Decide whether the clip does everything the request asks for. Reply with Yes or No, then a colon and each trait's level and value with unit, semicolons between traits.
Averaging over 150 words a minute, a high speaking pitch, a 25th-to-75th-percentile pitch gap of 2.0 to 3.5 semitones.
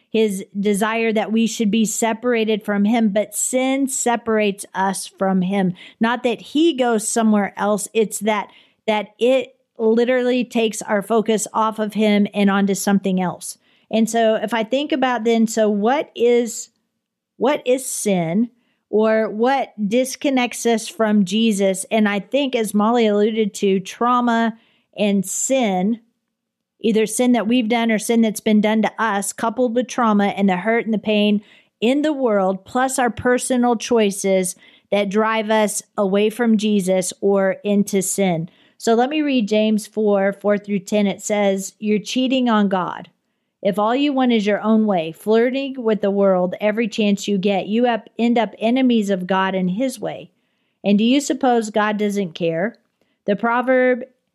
Yes: average, 170 wpm; high, 220 Hz; average, 2.8 semitones